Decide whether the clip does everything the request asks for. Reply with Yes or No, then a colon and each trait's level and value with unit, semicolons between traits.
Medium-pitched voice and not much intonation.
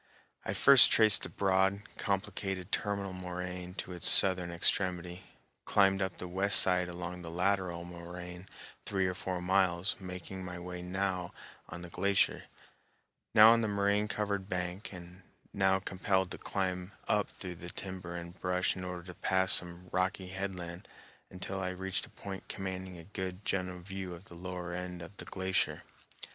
No: very low, 90 Hz; narrow, 1.4 semitones